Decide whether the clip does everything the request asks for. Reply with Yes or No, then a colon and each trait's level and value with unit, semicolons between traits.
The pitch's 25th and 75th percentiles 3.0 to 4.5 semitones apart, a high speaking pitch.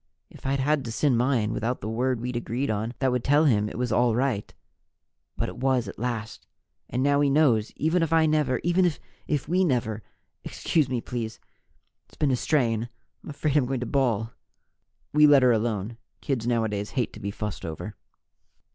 No: average, 4.0 semitones; low, 125 Hz